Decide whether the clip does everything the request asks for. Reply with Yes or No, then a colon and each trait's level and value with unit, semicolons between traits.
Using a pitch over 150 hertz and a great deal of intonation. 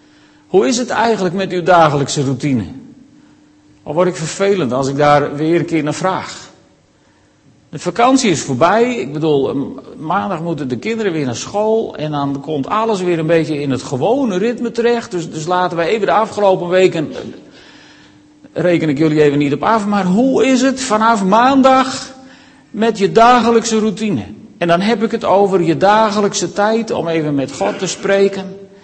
Yes: high, 190 Hz; wide, 6.2 semitones